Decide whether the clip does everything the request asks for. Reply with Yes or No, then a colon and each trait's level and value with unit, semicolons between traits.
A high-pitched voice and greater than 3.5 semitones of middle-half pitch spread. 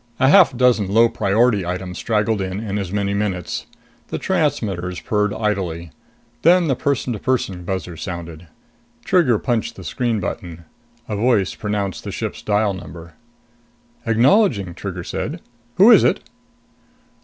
No: low, 105 Hz; average, 4.5 semitones